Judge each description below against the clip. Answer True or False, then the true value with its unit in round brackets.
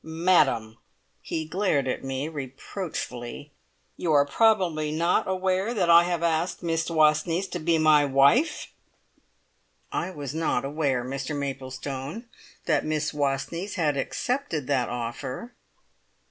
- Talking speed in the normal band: False (125 wpm)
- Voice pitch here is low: False (155 Hz)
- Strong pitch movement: False (4.0 semitones)